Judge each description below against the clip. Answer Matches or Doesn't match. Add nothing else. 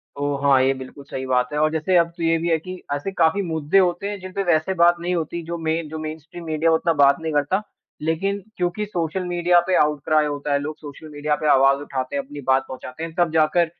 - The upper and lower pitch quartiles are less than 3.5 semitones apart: Matches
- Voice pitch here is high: Doesn't match